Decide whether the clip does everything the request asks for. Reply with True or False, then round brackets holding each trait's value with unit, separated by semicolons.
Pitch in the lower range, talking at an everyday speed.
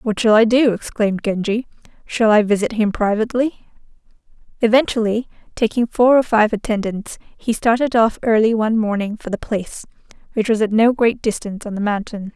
False (220 Hz; 170 wpm)